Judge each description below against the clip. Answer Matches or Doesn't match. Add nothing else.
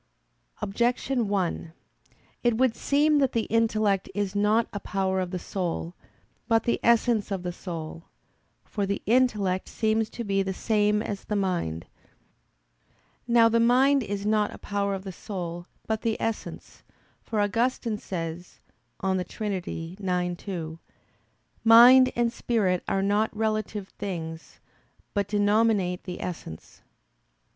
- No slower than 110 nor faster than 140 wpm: Matches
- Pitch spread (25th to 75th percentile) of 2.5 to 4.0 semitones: Matches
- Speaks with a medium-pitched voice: Doesn't match